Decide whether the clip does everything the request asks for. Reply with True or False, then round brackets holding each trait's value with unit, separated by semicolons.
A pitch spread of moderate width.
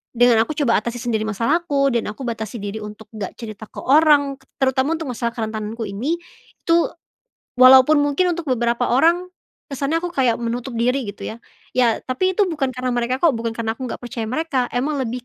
True (3.7 semitones)